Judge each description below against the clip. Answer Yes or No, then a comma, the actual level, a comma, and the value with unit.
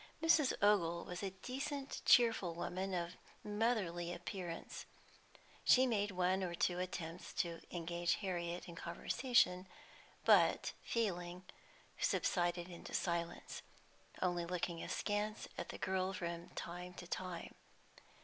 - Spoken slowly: Yes, slow, 120 wpm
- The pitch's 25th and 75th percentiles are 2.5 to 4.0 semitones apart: Yes, average, 3.0 semitones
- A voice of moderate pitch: Yes, medium, 180 Hz